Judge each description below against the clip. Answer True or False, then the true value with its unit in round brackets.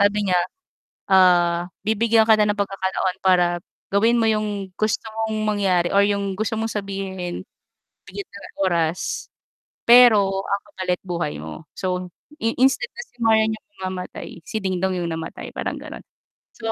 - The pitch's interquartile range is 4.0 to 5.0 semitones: False (3.2 semitones)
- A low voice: False (195 Hz)